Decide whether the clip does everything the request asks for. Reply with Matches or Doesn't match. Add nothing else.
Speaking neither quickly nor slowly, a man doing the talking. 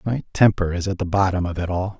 Doesn't match